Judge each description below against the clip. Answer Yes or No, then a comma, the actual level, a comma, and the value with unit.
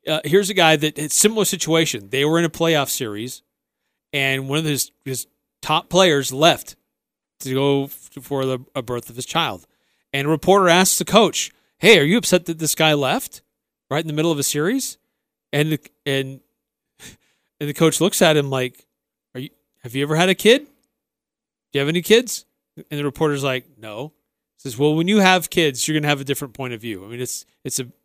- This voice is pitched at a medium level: Yes, medium, 150 Hz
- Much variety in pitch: No, average, 3.7 semitones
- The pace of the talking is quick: Yes, fast, 220 wpm